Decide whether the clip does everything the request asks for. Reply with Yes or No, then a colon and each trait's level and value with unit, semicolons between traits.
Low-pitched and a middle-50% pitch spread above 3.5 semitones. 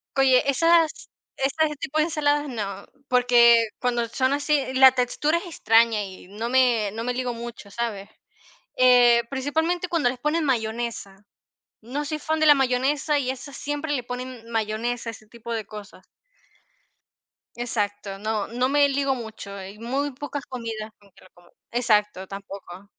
No: high, 245 Hz; average, 4.3 semitones